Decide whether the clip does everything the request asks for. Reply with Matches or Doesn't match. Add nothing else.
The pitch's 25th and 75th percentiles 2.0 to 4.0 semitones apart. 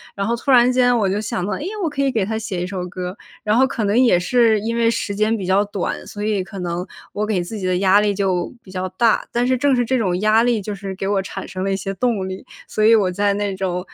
Matches